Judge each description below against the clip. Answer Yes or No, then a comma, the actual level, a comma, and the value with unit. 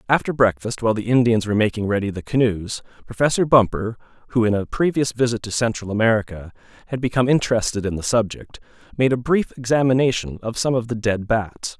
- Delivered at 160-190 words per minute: Yes, average, 185 wpm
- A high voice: No, low, 115 Hz